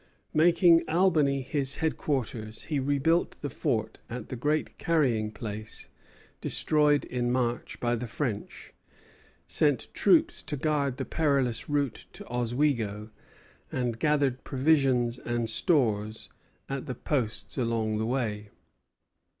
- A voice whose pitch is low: Yes, low, 130 Hz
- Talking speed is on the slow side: Yes, slow, 120 wpm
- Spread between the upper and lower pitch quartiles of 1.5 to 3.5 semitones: No, average, 4.3 semitones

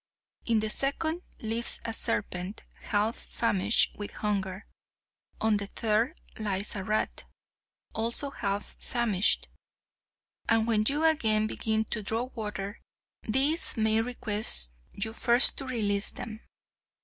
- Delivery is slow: Yes, slow, 125 wpm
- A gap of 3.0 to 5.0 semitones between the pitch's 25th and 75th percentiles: No, narrow, 2.4 semitones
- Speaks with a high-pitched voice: Yes, high, 220 Hz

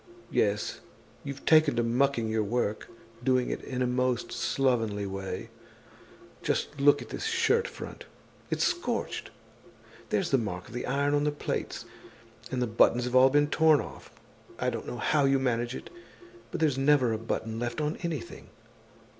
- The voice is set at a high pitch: No, low, 130 Hz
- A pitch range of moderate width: Yes, average, 3.9 semitones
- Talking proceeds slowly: No, average, 165 wpm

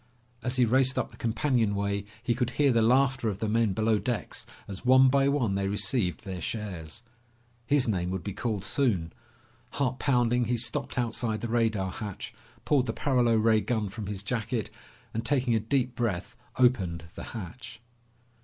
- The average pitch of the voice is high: No, low, 115 Hz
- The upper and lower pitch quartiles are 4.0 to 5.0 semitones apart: No, average, 3.6 semitones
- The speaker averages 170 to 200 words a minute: Yes, average, 175 wpm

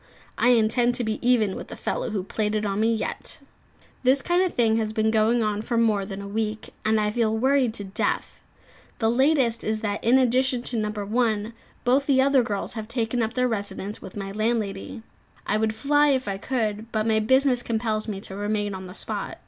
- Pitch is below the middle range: No, high, 220 Hz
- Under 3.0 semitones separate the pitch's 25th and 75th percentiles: Yes, narrow, 2.6 semitones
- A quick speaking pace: Yes, fast, 215 wpm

